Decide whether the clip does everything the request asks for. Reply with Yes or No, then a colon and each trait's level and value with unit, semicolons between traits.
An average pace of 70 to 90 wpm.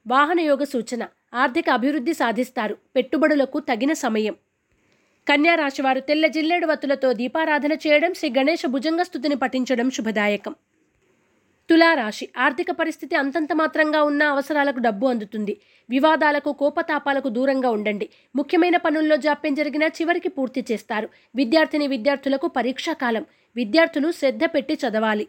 No: average, 110 wpm